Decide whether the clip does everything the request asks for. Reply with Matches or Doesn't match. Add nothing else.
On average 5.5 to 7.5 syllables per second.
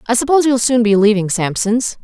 Matches